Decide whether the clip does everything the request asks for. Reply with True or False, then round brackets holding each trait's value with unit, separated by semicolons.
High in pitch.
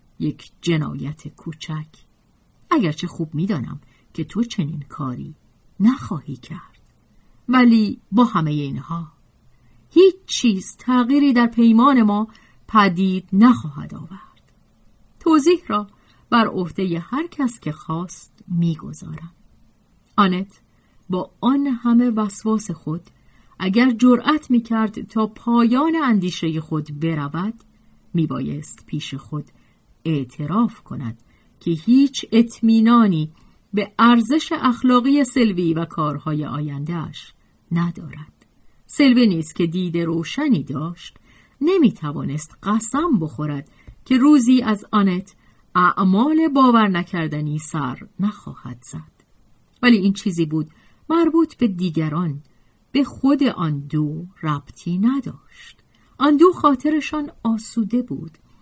True (195 Hz)